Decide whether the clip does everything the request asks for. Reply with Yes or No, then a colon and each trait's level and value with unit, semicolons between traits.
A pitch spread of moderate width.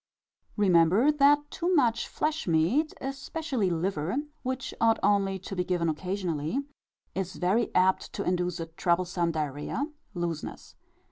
No: wide, 7.2 semitones